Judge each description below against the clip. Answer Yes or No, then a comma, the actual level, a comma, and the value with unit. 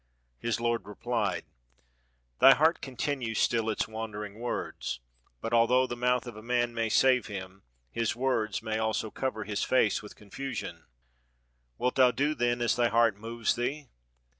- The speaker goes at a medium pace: Yes, average, 165 wpm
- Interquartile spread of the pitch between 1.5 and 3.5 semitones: Yes, narrow, 2.4 semitones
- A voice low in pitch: Yes, low, 115 Hz